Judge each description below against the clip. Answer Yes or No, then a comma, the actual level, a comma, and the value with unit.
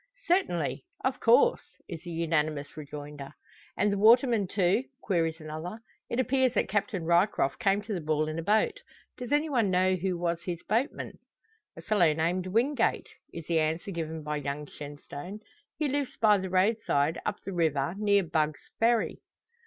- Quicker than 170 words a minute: No, average, 165 wpm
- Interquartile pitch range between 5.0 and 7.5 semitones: Yes, wide, 5.6 semitones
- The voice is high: No, medium, 180 Hz